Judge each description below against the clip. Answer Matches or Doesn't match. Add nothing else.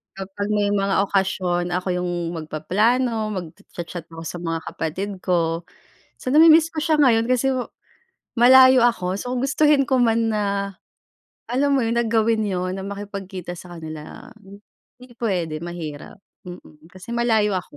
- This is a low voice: Doesn't match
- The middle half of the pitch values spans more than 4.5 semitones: Matches